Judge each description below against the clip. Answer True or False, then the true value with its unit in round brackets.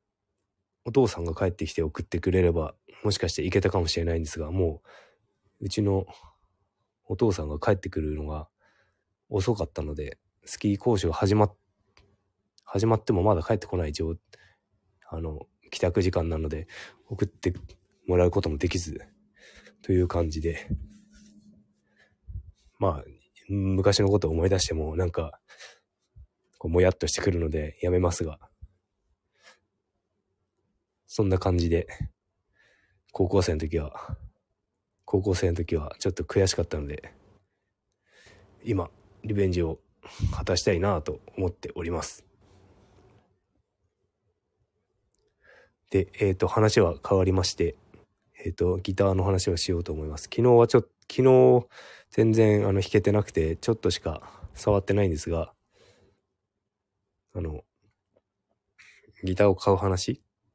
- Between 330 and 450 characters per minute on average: False (260 characters per minute)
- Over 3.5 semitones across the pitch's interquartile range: False (3.0 semitones)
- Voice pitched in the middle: False (95 Hz)